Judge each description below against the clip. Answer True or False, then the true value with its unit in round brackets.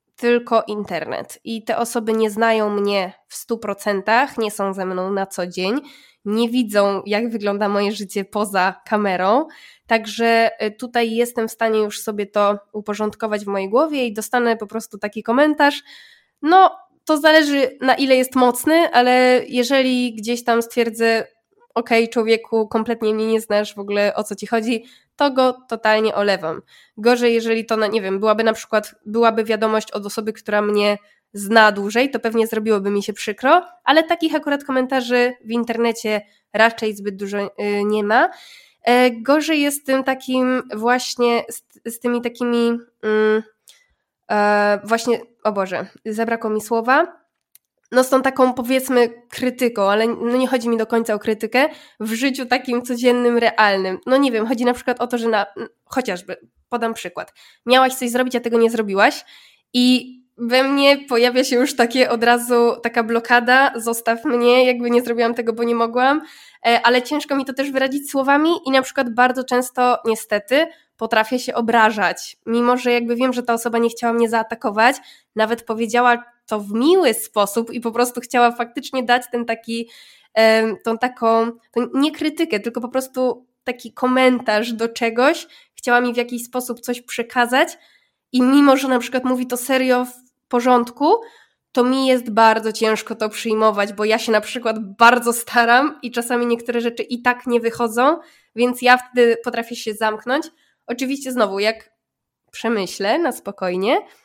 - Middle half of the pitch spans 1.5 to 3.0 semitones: True (2.5 semitones)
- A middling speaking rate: False (165 wpm)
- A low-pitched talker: False (235 Hz)